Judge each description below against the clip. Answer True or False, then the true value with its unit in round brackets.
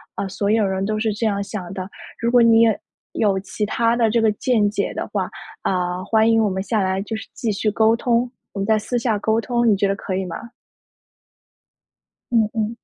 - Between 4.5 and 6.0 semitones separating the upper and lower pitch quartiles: False (2.5 semitones)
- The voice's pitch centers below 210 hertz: False (215 Hz)